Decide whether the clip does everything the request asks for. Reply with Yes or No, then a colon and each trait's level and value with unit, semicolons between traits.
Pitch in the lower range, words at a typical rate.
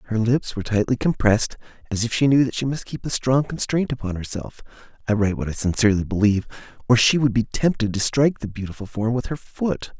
No: low, 120 Hz; fast, 210 wpm